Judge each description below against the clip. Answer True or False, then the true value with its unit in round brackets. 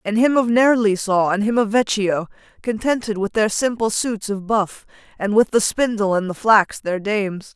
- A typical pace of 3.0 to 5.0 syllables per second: True (4.7 syllables/s)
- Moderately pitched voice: False (210 Hz)